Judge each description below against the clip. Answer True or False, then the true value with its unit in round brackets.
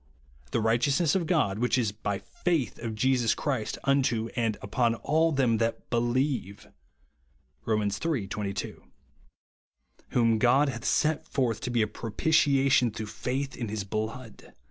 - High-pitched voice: False (120 Hz)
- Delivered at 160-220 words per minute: False (145 wpm)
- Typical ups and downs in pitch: True (3.9 semitones)